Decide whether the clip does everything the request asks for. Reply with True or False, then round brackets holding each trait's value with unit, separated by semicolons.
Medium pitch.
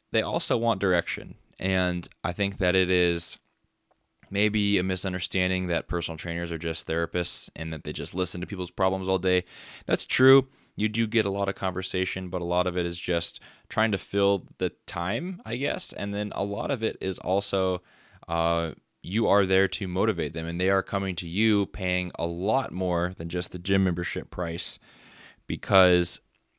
False (90 Hz)